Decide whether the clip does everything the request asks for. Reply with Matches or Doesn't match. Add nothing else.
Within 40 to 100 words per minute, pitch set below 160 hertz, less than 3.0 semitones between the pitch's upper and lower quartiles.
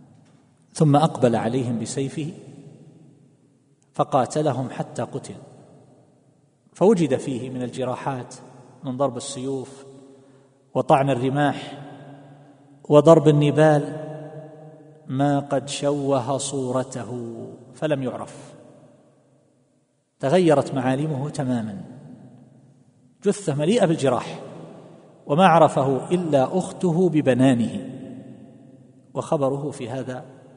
Matches